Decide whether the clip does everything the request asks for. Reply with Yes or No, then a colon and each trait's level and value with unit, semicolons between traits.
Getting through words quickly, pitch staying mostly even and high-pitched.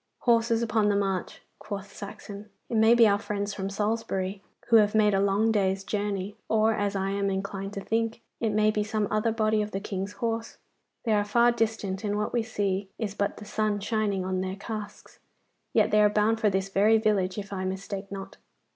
Yes: fast, 210 wpm; narrow, 1.8 semitones; high, 205 Hz